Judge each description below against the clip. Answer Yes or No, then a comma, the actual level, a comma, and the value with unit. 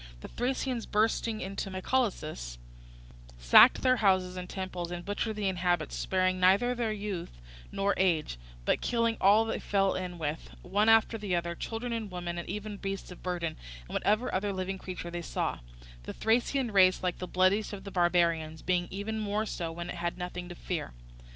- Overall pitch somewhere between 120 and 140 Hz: No, high, 190 Hz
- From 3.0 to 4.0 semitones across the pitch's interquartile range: Yes, average, 3.4 semitones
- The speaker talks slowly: No, average, 180 wpm